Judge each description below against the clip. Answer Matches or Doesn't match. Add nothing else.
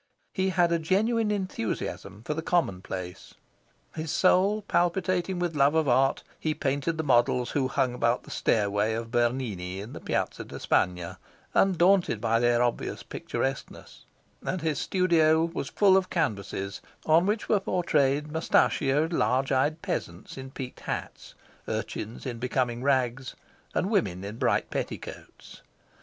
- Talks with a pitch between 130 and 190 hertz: Matches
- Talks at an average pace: Matches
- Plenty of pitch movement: Matches